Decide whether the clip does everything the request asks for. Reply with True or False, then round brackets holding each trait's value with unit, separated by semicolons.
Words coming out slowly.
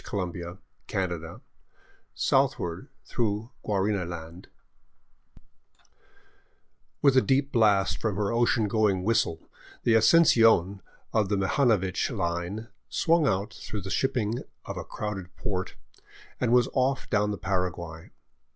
True (120 wpm)